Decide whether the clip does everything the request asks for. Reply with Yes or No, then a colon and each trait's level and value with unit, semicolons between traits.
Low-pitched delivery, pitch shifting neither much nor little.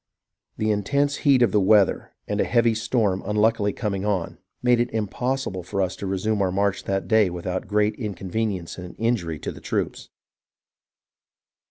Yes: low, 105 Hz; average, 3.2 semitones